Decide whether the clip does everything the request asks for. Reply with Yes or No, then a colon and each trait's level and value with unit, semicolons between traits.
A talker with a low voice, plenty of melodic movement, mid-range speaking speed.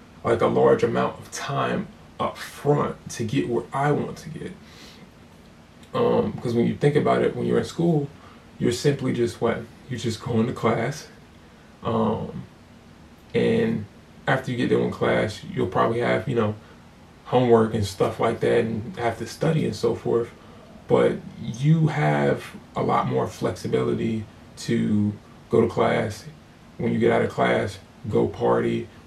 Yes: low, 115 Hz; wide, 6.7 semitones; average, 165 wpm